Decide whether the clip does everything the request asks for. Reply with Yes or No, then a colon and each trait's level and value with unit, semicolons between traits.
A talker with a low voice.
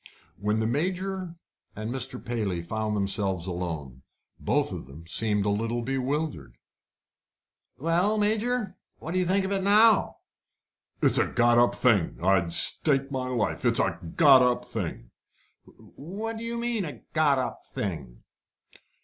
Yes: low, 125 Hz